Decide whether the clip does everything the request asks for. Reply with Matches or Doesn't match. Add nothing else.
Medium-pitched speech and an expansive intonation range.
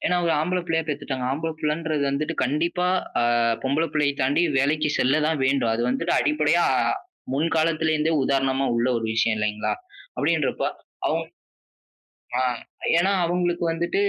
Doesn't match